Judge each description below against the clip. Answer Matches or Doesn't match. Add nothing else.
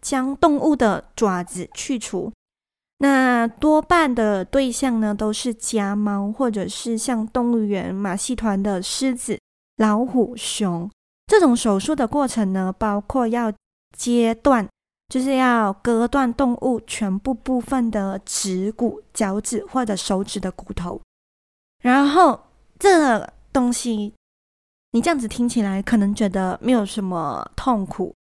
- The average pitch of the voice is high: Matches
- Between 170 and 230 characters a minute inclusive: Matches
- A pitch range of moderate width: Matches